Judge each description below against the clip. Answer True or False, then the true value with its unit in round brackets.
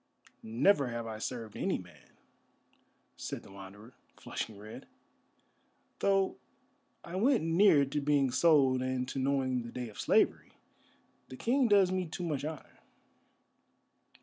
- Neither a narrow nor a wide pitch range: False (6.1 semitones)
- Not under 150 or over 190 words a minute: False (135 wpm)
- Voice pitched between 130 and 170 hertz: True (135 Hz)